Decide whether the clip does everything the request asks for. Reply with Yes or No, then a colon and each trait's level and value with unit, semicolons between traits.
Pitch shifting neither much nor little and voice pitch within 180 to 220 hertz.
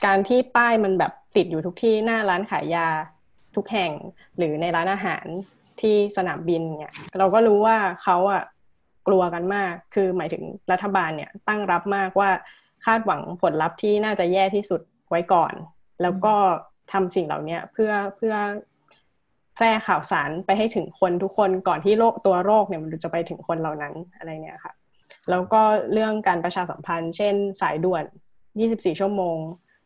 Yes: average, 3.3 semitones; high, 190 Hz